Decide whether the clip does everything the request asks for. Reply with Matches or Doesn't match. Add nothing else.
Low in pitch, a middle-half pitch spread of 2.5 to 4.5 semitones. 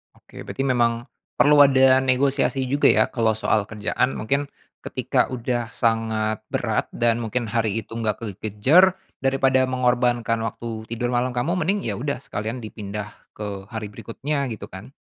Matches